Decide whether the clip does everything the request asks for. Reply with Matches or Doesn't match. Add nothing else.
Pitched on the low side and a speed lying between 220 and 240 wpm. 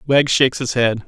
Matches